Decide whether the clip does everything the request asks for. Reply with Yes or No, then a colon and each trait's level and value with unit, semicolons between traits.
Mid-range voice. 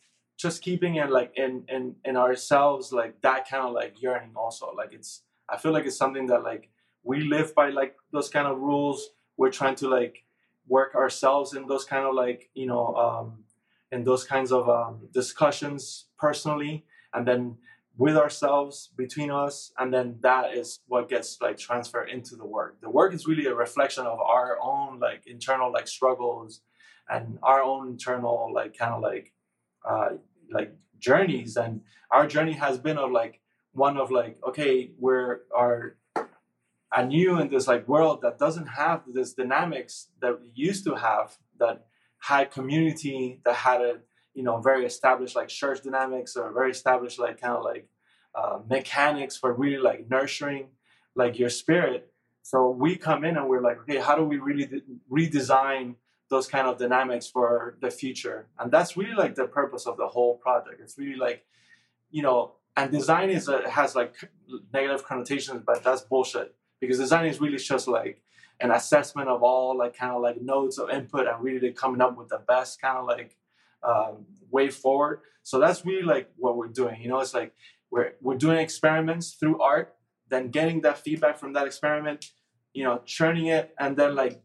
No: low, 130 Hz